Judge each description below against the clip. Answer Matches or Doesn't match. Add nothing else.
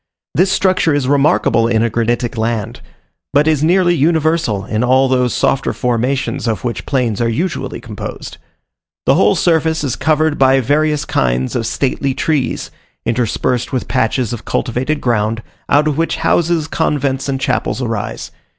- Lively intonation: Doesn't match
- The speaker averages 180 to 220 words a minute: Doesn't match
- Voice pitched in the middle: Doesn't match